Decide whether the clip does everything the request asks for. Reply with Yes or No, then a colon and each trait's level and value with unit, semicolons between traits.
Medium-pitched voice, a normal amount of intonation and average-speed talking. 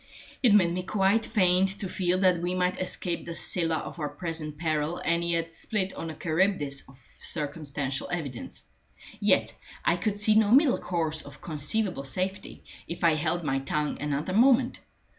Yes: medium, 170 Hz; average, 3.9 semitones; average, 170 wpm